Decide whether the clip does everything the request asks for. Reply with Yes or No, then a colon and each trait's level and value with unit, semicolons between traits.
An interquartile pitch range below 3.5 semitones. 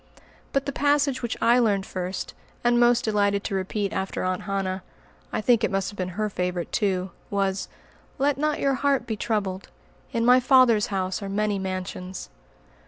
No: average, 4.1 semitones